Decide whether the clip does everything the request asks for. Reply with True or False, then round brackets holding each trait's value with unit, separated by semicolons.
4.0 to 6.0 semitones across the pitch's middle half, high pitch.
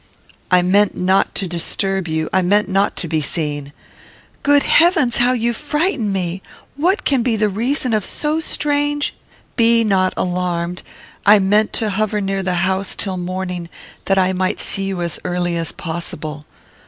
True (4.3 semitones; 195 Hz)